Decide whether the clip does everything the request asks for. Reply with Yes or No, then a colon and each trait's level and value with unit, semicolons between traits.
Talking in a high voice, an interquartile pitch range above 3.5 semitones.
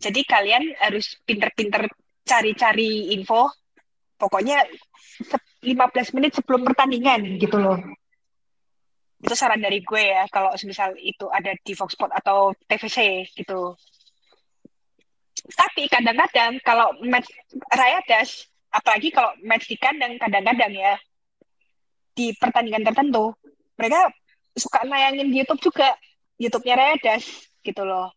Yes: high, 230 Hz; average, 4.9 semitones